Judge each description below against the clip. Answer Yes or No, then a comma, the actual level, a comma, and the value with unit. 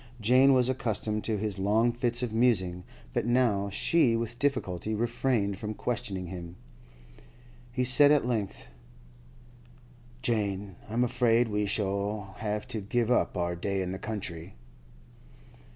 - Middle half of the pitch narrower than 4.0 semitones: Yes, average, 3.5 semitones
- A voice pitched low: Yes, low, 110 Hz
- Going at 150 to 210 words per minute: No, slow, 135 wpm